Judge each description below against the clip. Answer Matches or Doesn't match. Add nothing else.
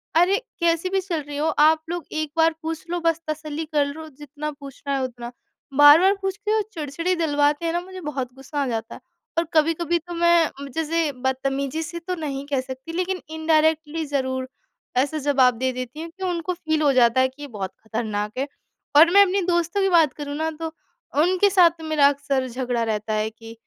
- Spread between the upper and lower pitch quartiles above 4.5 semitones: Doesn't match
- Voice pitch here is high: Matches